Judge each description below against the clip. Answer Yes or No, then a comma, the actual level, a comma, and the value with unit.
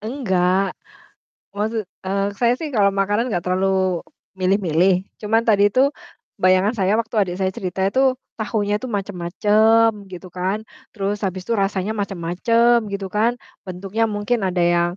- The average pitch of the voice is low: No, high, 200 Hz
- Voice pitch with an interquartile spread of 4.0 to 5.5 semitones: No, average, 2.9 semitones